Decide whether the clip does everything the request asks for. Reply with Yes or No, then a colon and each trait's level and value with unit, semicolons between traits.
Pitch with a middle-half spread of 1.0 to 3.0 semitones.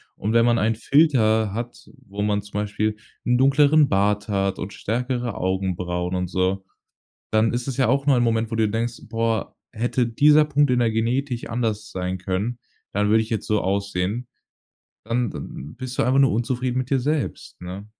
No: average, 3.5 semitones